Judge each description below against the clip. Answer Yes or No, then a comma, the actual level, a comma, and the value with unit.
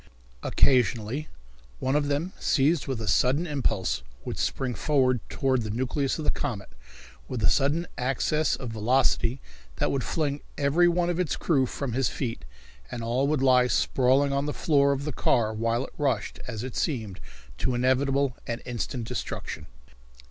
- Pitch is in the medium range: No, low, 130 Hz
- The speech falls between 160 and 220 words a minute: Yes, average, 170 wpm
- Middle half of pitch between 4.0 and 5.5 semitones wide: No, average, 3.0 semitones